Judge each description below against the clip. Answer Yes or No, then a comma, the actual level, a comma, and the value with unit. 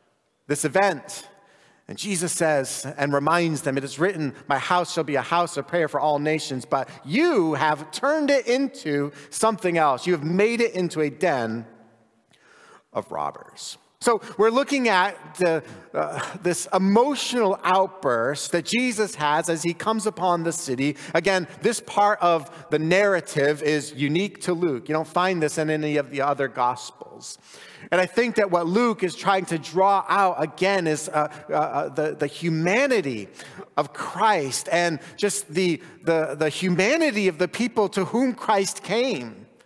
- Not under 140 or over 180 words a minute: Yes, average, 165 wpm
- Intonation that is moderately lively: Yes, average, 4.8 semitones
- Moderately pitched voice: Yes, medium, 175 Hz